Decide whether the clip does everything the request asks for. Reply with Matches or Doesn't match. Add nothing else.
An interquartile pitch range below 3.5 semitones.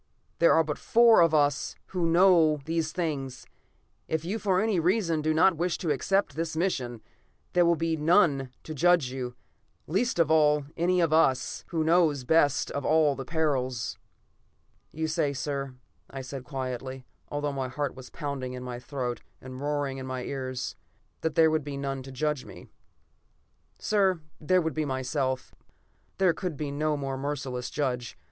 Doesn't match